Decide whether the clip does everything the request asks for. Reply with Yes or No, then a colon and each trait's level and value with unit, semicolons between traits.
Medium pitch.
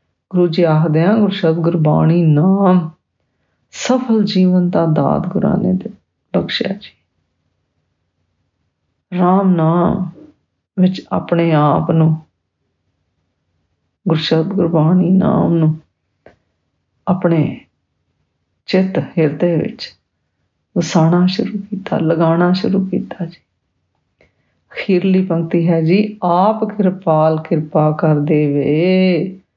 Yes: medium, 170 Hz